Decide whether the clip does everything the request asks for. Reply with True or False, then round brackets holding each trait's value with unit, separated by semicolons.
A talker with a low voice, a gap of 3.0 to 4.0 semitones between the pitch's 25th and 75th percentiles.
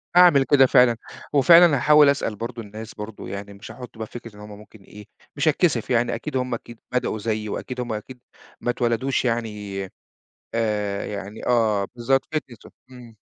True (115 Hz; 3.4 semitones)